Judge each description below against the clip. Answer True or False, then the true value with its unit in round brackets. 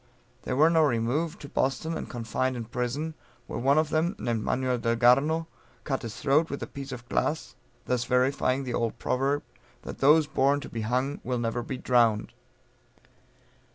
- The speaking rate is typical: True (175 wpm)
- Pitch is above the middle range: False (130 Hz)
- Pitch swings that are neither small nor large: True (3.3 semitones)